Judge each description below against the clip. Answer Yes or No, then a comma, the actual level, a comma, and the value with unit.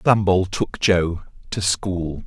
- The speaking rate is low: Yes, slow, 130 wpm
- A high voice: No, very low, 95 Hz